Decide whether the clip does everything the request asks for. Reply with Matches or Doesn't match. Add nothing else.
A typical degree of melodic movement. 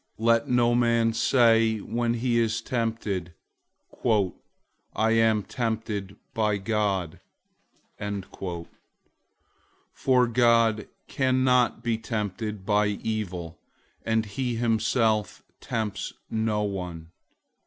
Doesn't match